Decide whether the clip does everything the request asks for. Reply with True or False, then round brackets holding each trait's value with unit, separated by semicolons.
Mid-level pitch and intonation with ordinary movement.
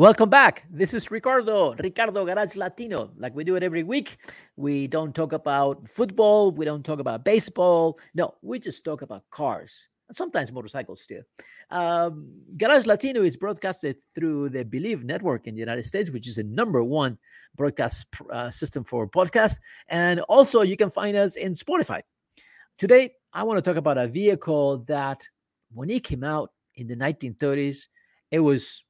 False (165 Hz; 6.6 semitones)